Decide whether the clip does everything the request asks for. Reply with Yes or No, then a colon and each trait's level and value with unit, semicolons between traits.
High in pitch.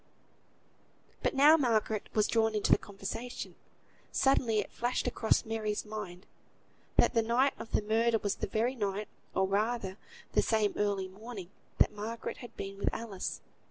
Yes: high, 220 Hz